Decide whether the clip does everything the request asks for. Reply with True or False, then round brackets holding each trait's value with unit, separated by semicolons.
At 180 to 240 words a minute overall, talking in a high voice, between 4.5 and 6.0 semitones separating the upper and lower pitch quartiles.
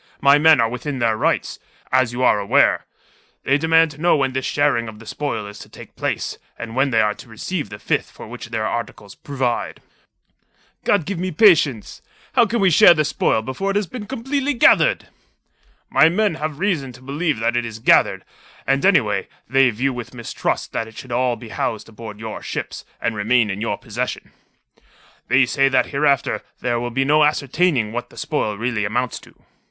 False (200 wpm; 130 Hz; 5.2 semitones)